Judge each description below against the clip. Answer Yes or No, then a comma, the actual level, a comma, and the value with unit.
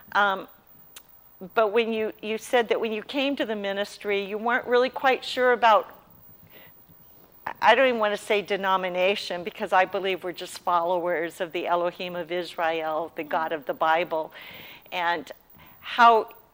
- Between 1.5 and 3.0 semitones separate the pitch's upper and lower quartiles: No, average, 4.1 semitones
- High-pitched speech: Yes, high, 200 Hz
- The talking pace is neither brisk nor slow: Yes, average, 160 wpm